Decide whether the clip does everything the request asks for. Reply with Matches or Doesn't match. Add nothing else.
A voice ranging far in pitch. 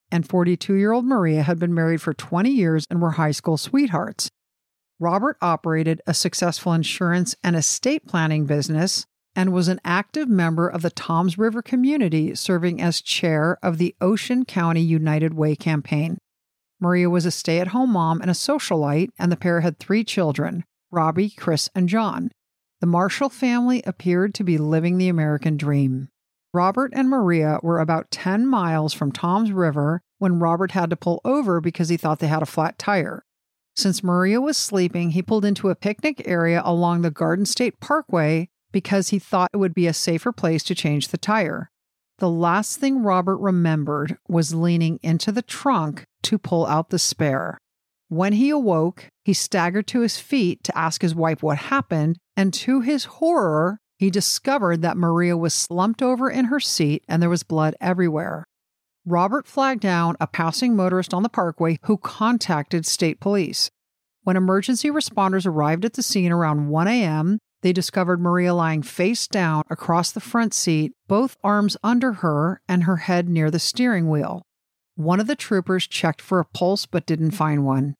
Doesn't match